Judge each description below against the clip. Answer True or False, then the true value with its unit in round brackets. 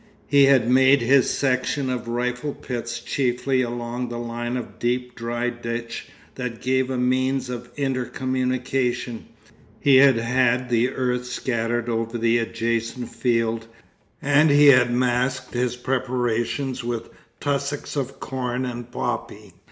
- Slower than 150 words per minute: True (135 wpm)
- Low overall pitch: True (125 Hz)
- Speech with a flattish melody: True (1.7 semitones)